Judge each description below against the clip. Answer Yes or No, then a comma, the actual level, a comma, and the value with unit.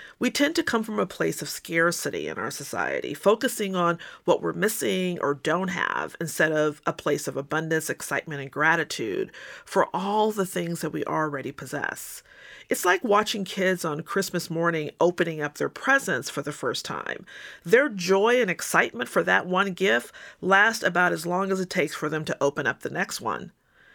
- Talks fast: No, average, 190 wpm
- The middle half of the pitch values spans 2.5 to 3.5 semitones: No, average, 4.1 semitones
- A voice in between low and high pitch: Yes, medium, 175 Hz